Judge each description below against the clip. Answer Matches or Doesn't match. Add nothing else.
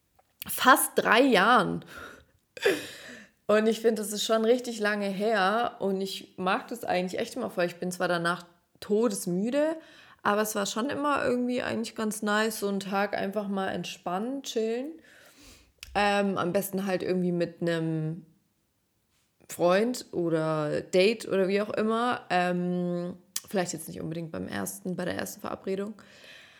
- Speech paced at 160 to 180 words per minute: Doesn't match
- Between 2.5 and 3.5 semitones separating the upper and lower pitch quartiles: Doesn't match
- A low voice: Doesn't match